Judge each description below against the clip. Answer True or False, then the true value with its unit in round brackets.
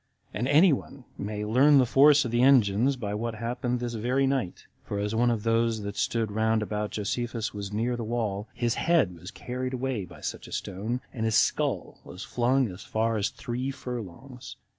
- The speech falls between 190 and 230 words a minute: True (200 wpm)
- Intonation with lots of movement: False (3.2 semitones)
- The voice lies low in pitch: True (115 Hz)